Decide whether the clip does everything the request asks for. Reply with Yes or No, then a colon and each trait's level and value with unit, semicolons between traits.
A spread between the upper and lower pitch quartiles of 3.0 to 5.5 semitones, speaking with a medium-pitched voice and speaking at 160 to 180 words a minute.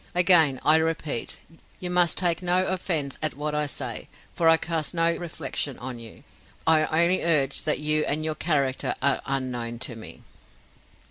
Yes: average, 3.6 semitones; medium, 155 Hz; average, 170 wpm